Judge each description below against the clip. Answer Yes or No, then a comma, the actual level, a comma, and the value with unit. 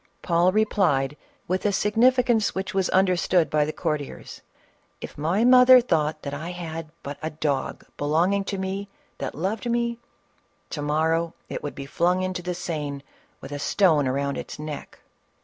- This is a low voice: No, medium, 170 Hz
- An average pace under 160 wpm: No, average, 165 wpm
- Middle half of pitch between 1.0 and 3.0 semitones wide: No, average, 4.7 semitones